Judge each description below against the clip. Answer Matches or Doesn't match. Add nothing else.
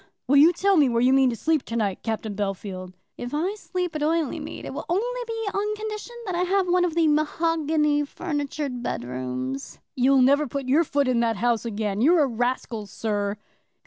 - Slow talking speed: Doesn't match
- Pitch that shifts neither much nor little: Doesn't match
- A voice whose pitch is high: Matches